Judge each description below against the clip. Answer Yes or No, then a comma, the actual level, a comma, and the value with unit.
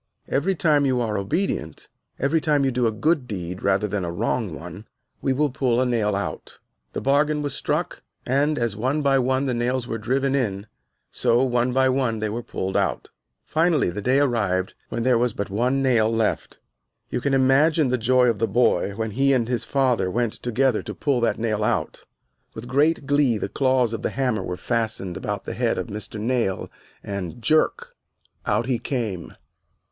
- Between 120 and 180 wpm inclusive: No, average, 195 wpm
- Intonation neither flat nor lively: Yes, average, 4.0 semitones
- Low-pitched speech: Yes, low, 120 Hz